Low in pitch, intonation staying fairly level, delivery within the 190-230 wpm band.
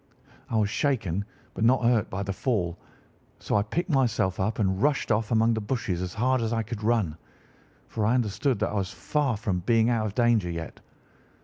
No: low, 110 Hz; average, 3.5 semitones; fast, 205 wpm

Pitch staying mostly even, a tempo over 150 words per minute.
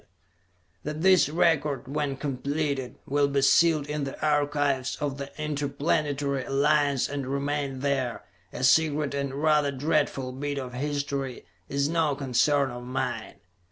No: narrow, 1.7 semitones; average, 140 wpm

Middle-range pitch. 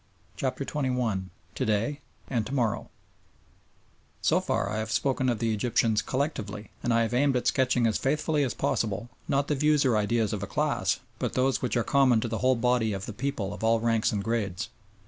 No: low, 120 Hz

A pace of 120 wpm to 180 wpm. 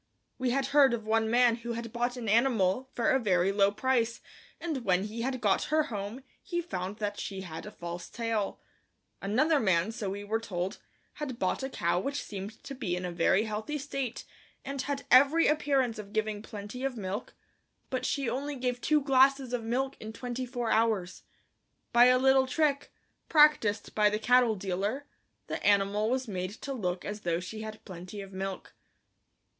No: average, 190 wpm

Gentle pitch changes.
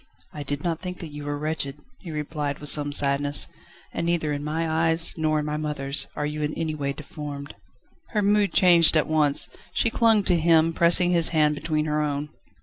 Yes: narrow, 2.1 semitones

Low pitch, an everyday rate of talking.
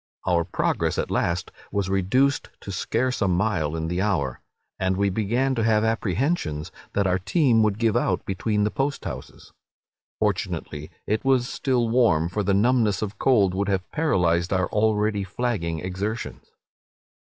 Yes: low, 100 Hz; average, 160 wpm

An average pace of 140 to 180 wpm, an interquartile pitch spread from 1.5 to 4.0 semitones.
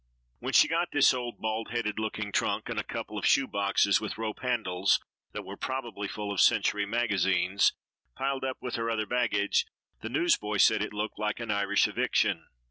No: average, 190 wpm; average, 2.9 semitones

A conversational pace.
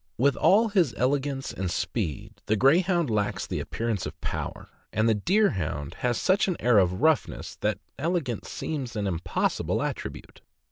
Yes: average, 155 wpm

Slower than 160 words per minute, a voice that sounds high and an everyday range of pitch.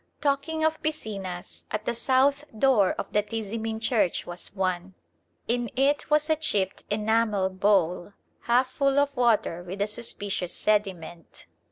No: average, 145 wpm; high, 220 Hz; wide, 5.9 semitones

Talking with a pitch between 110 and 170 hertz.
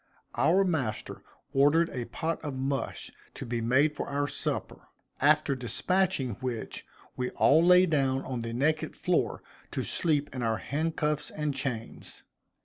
Yes: medium, 140 Hz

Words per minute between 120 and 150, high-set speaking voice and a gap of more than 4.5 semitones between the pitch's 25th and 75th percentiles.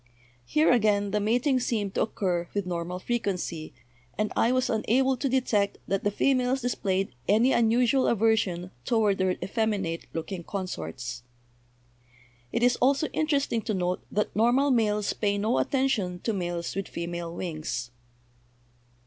Yes: average, 140 wpm; high, 210 Hz; average, 5.1 semitones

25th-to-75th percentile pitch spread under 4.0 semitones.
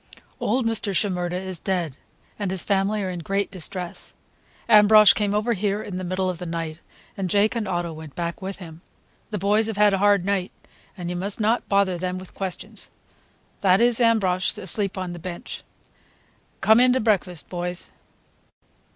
Yes: average, 2.7 semitones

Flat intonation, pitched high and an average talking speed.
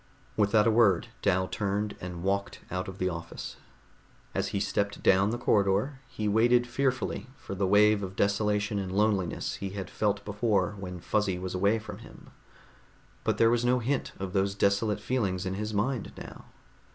No: narrow, 2.3 semitones; low, 100 Hz; average, 175 wpm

